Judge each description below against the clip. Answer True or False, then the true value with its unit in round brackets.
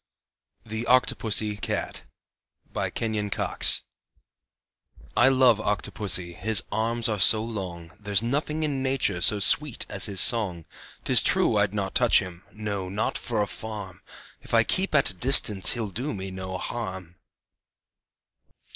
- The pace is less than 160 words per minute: True (140 wpm)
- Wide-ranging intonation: False (3.7 semitones)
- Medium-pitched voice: False (105 Hz)